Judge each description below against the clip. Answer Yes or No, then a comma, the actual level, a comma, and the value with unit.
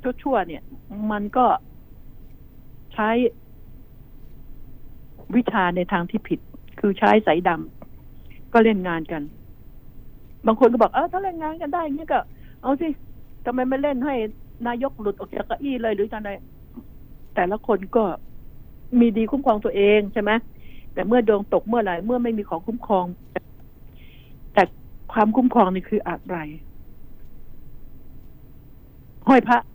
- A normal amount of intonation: Yes, average, 3.8 semitones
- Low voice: No, high, 220 Hz